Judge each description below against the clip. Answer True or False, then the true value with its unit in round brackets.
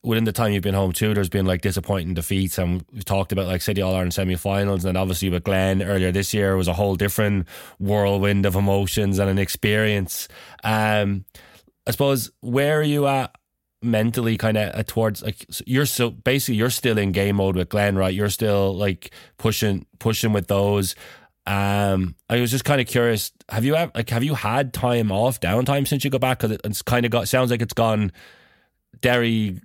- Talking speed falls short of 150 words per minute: False (205 wpm)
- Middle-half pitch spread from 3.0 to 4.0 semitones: True (3.3 semitones)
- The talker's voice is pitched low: True (105 Hz)